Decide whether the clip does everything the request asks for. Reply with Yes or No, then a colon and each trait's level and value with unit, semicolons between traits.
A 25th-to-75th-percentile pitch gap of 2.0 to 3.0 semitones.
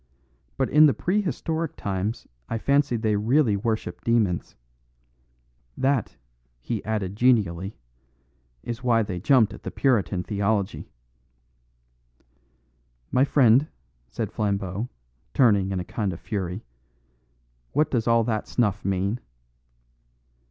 No: average, 4.1 semitones